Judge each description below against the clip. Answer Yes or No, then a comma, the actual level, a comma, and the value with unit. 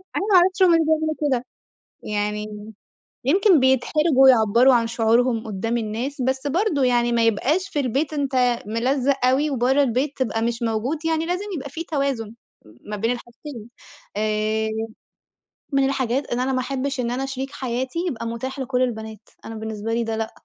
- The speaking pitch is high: Yes, very high, 255 Hz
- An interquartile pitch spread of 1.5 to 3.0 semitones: No, average, 3.6 semitones